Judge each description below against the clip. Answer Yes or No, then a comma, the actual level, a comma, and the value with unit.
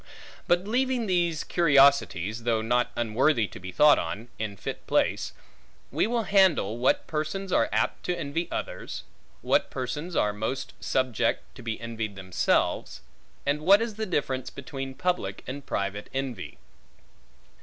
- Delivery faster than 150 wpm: No, average, 145 wpm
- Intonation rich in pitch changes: Yes, wide, 7.6 semitones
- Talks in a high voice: No, low, 135 Hz